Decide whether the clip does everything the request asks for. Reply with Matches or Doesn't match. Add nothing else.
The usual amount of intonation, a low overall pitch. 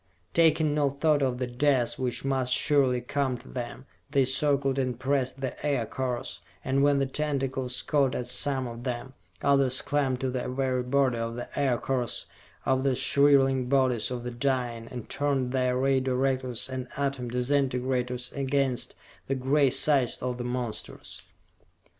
Doesn't match